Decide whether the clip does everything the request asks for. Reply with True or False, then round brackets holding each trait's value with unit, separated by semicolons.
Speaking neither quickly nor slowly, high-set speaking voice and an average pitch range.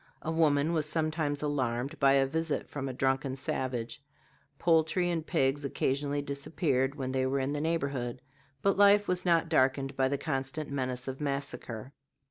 False (165 wpm; 140 Hz; 3.0 semitones)